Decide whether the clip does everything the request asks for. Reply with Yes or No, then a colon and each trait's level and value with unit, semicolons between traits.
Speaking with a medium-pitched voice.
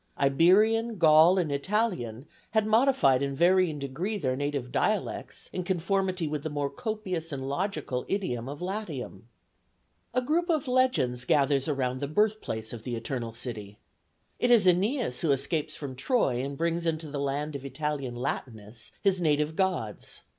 Yes: medium, 155 Hz